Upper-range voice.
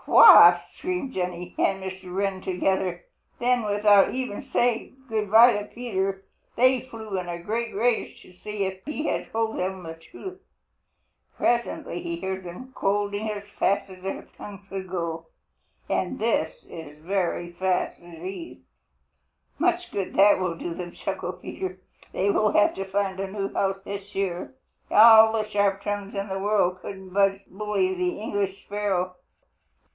Yes: high, 195 Hz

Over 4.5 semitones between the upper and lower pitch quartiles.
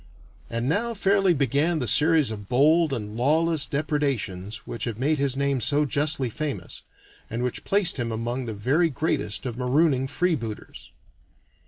Yes: average, 4.9 semitones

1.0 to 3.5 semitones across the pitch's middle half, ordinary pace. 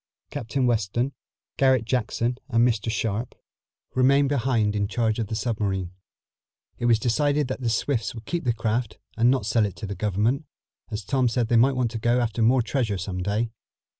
Yes: average, 2.8 semitones; average, 190 wpm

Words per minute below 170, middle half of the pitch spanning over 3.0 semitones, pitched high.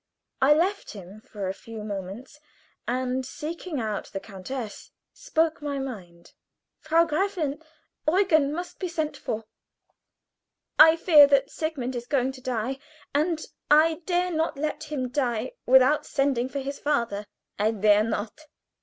Yes: average, 145 wpm; wide, 5.5 semitones; very high, 275 Hz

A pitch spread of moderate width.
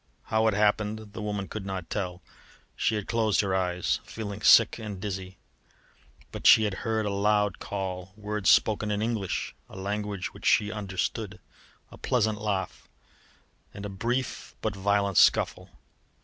No: narrow, 2.0 semitones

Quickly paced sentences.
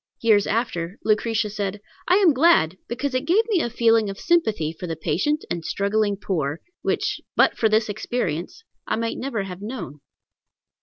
No: average, 170 wpm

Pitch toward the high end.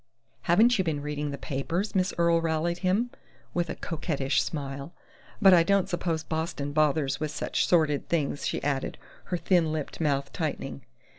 No: medium, 160 Hz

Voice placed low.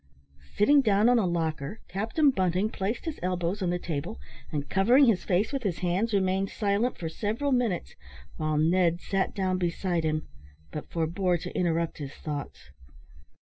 No: medium, 185 Hz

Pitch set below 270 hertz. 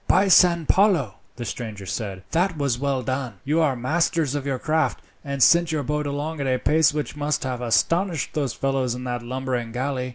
Yes: medium, 140 Hz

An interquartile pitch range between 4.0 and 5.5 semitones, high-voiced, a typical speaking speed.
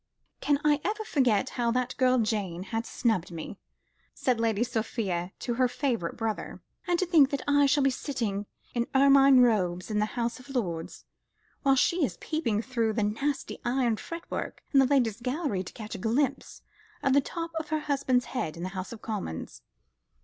Yes: average, 4.6 semitones; high, 245 Hz; average, 185 wpm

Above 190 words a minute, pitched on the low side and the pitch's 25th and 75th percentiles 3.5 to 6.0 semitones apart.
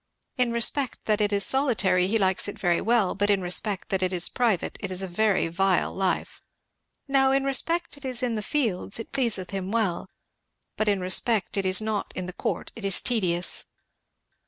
No: average, 200 wpm; high, 205 Hz; average, 4.0 semitones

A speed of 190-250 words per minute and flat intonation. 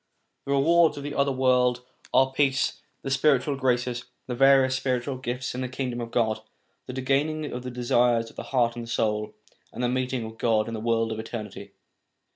Yes: average, 200 wpm; narrow, 2.3 semitones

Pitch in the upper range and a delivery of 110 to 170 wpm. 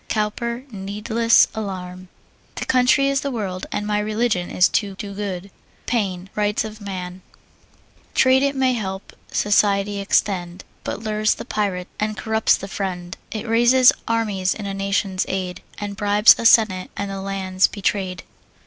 Yes: high, 205 Hz; average, 155 wpm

